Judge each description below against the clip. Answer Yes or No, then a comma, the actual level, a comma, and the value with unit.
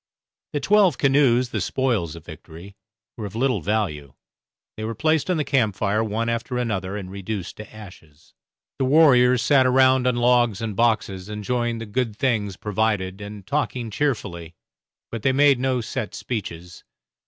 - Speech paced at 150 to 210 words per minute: Yes, average, 165 wpm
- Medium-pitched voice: No, low, 115 Hz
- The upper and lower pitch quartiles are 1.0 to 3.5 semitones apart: No, average, 4.4 semitones